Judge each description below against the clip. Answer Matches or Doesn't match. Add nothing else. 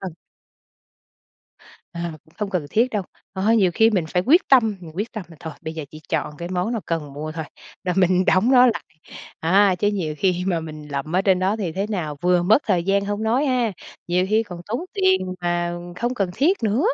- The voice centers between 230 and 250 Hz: Doesn't match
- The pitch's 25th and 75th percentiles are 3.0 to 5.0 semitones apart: Matches